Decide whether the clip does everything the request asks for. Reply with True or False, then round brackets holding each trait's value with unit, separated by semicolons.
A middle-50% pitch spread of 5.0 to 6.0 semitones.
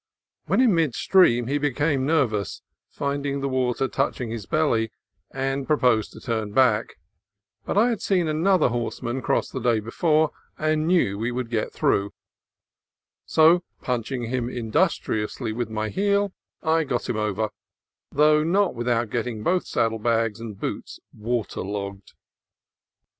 True (5.4 semitones)